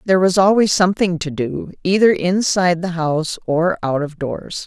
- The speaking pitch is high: No, medium, 175 Hz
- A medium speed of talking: Yes, average, 180 wpm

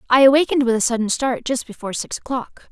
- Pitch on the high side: Yes, very high, 250 Hz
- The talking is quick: Yes, fast, 220 wpm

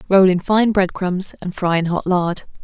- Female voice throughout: Yes, female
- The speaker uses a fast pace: Yes, fast, 230 wpm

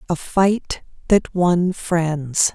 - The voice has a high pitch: No, medium, 175 Hz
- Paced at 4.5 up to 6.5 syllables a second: No, 2.4 syllables/s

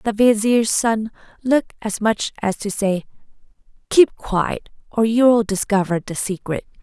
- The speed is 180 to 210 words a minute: No, average, 140 wpm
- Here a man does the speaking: No, female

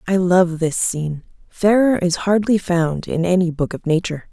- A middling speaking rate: Yes, average, 180 wpm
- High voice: No, medium, 180 Hz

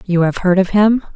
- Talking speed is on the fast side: Yes, fast, 260 wpm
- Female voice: Yes, female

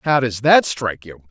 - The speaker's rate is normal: No, fast, 230 wpm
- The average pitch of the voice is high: No, low, 120 Hz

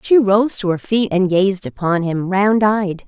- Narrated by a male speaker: No, female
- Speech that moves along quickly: Yes, fast, 215 wpm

